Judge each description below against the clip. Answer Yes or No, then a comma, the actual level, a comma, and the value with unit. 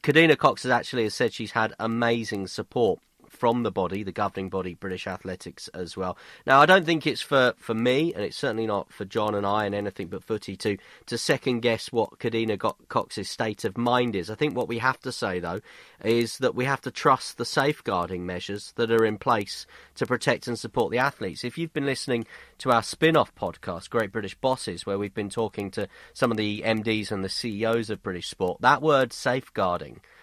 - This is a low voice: Yes, low, 115 Hz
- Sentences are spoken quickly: Yes, fast, 210 wpm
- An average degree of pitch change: Yes, average, 3.6 semitones